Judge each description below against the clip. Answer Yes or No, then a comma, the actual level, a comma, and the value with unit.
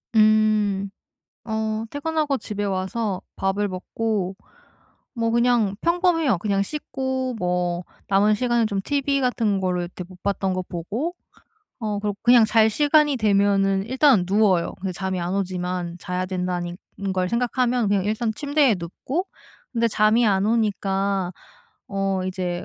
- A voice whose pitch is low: No, high, 205 Hz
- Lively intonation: No, average, 4.0 semitones